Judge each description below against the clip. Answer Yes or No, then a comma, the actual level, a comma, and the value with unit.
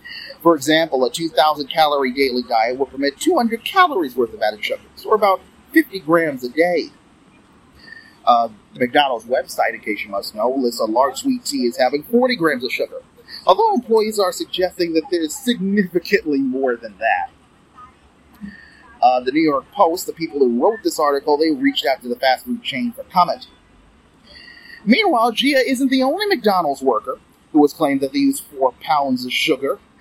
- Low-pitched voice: No, high, 195 Hz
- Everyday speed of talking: Yes, average, 185 wpm